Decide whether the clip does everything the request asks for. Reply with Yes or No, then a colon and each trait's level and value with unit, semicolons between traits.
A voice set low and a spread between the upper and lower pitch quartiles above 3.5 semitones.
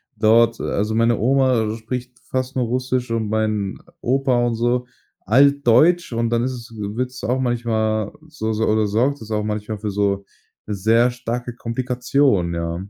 No: low, 115 Hz; narrow, 2.6 semitones